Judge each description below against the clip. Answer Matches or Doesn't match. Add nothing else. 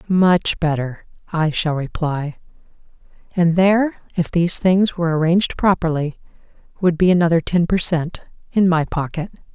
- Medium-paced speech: Doesn't match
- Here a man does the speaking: Doesn't match